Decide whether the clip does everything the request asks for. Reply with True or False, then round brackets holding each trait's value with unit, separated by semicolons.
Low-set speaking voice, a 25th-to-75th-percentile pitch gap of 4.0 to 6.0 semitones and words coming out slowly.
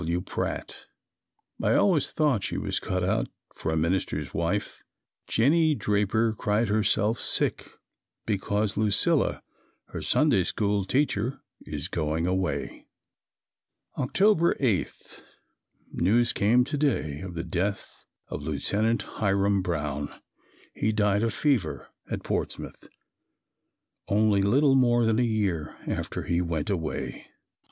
True (105 Hz; 4.8 semitones; 120 wpm)